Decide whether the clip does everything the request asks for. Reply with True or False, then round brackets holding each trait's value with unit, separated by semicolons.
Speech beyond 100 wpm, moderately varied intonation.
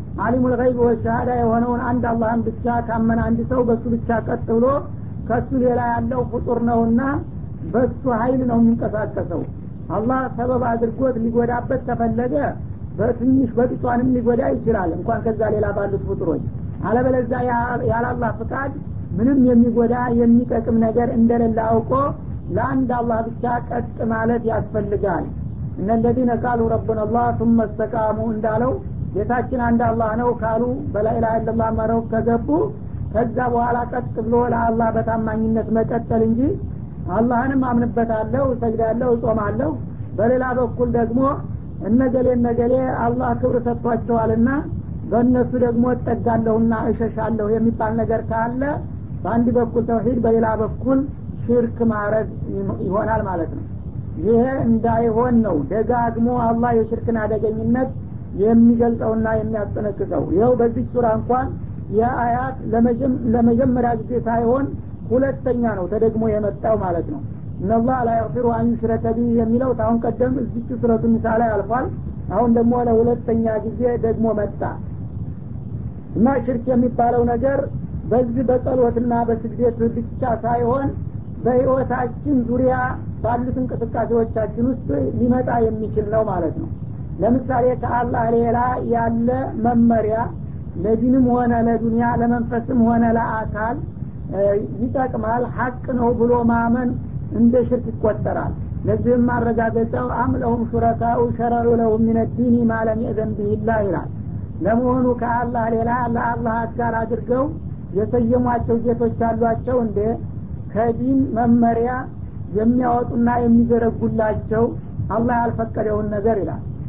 False (110 wpm; 1.3 semitones)